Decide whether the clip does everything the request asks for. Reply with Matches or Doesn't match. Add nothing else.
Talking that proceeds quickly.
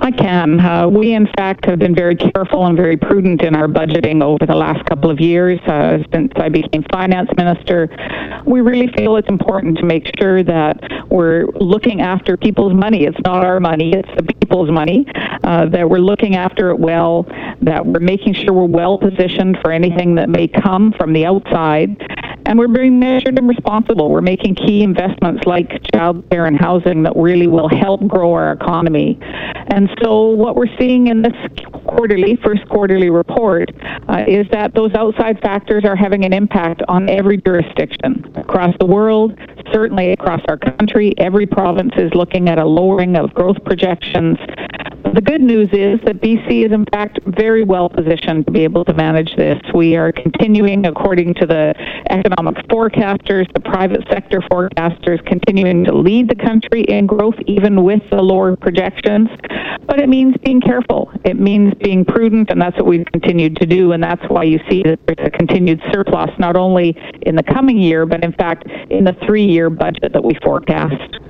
Doesn't match